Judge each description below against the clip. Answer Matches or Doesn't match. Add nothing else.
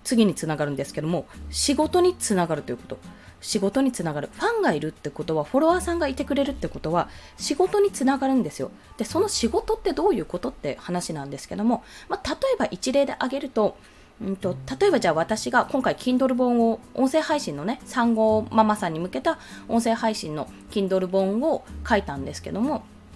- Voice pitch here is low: Doesn't match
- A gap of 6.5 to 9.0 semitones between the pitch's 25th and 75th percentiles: Matches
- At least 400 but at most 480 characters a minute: Matches